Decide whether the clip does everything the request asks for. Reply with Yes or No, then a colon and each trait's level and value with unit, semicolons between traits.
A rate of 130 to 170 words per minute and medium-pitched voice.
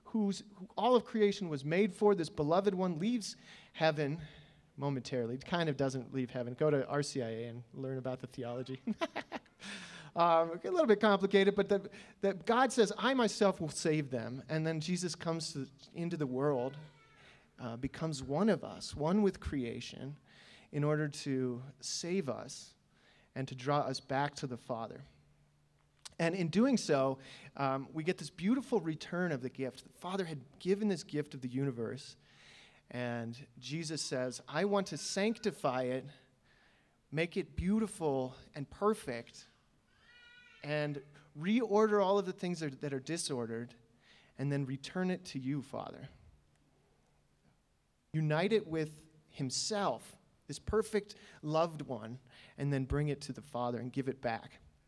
Yes: average, 160 wpm; medium, 150 Hz